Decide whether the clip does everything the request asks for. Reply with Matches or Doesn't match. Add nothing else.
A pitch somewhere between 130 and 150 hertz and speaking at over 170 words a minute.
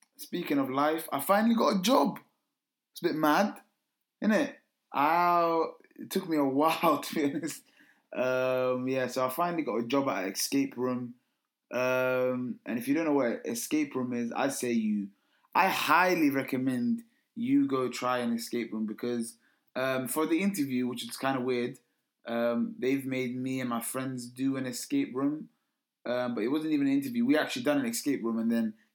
Matches